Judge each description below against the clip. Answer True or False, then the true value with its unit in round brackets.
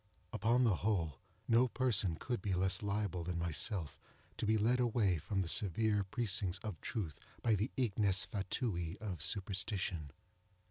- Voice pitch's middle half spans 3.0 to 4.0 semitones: True (3.7 semitones)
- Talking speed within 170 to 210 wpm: False (150 wpm)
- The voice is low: True (100 Hz)